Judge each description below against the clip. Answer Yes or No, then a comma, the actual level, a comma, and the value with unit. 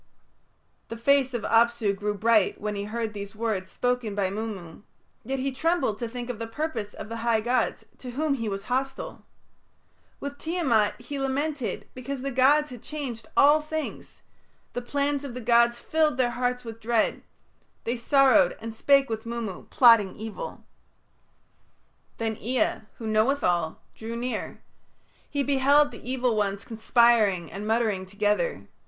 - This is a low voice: No, high, 235 Hz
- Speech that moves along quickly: No, average, 160 wpm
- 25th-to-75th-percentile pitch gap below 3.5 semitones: No, average, 3.8 semitones